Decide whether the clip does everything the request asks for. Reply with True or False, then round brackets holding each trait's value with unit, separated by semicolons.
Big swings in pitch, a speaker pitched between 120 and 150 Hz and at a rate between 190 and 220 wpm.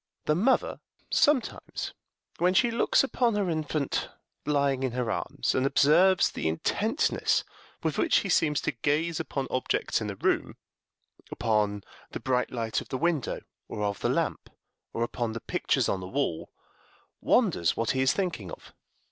False (6.6 semitones; 135 Hz; 165 wpm)